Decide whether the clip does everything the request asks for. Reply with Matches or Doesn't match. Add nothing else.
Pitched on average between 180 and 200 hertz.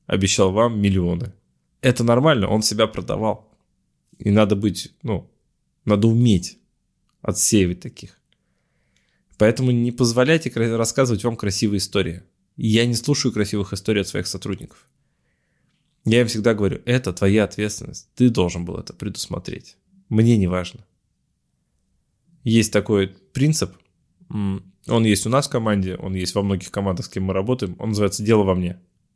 Doesn't match